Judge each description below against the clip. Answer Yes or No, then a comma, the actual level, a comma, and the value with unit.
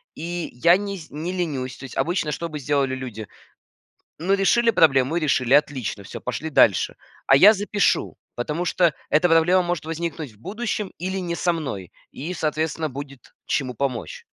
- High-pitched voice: No, medium, 160 Hz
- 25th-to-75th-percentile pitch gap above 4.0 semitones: Yes, average, 4.7 semitones